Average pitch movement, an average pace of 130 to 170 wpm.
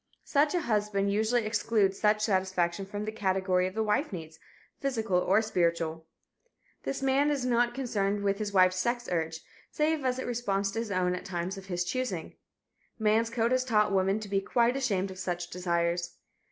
No: average, 4.2 semitones; average, 185 wpm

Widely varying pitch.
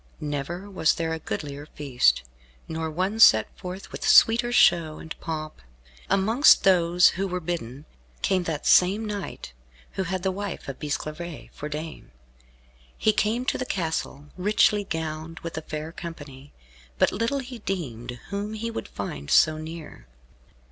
No: average, 4.5 semitones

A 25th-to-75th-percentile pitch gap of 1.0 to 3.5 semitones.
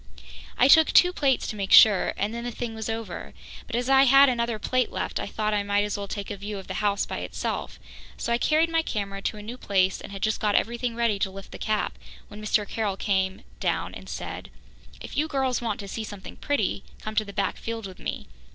Yes: average, 3.2 semitones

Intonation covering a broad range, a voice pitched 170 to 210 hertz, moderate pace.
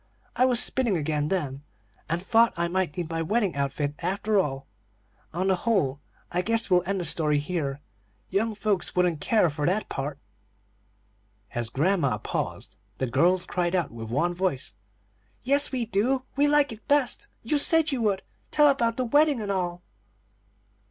Yes: wide, 7.1 semitones; medium, 185 Hz; average, 170 wpm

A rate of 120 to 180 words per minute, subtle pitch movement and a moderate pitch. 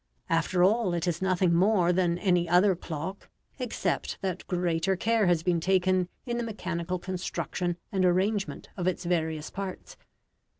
Yes: average, 155 wpm; narrow, 1.8 semitones; medium, 180 Hz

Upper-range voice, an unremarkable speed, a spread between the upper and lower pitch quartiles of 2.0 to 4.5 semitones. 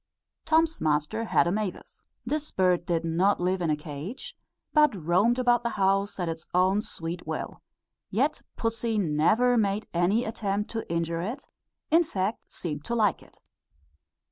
No: high, 195 Hz; average, 160 wpm; average, 5.3 semitones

